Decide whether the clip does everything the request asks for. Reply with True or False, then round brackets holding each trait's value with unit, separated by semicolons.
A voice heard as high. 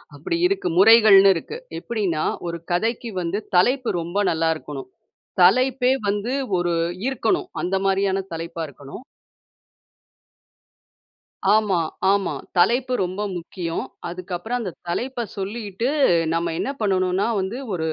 True (195 Hz)